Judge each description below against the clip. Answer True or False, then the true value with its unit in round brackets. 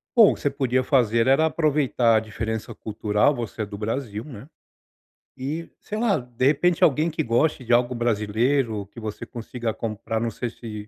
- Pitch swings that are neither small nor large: True (4.1 semitones)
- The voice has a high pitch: False (120 Hz)